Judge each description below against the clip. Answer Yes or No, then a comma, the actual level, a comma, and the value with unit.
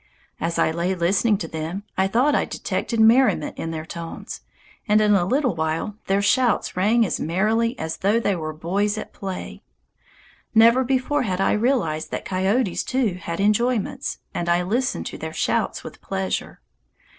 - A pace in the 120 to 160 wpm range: No, average, 170 wpm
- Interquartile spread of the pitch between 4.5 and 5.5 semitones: Yes, average, 5.2 semitones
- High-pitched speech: Yes, high, 200 Hz